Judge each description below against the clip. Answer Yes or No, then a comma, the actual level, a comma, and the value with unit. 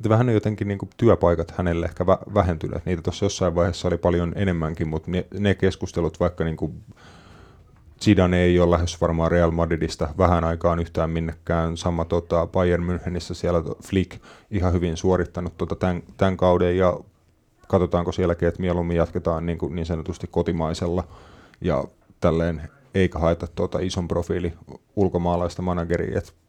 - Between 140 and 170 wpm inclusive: Yes, average, 150 wpm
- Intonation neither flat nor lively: No, narrow, 1.6 semitones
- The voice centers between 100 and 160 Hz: No, very low, 90 Hz